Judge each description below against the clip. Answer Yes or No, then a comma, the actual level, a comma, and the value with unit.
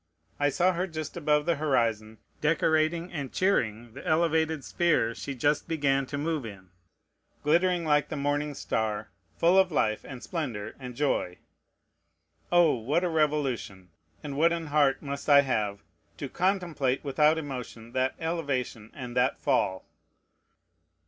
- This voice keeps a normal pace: Yes, average, 145 wpm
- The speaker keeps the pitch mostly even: No, average, 4.5 semitones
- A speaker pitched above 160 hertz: No, medium, 145 Hz